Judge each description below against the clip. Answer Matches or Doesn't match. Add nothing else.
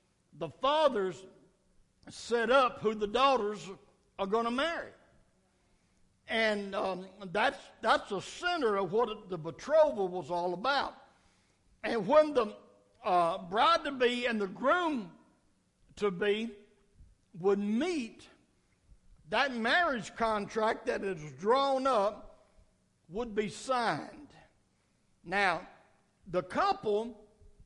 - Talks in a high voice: Matches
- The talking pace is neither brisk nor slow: Doesn't match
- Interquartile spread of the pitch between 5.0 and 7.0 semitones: Matches